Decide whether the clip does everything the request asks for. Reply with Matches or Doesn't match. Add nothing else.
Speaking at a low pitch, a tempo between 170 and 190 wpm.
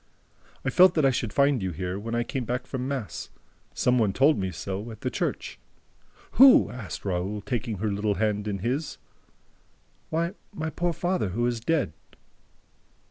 Matches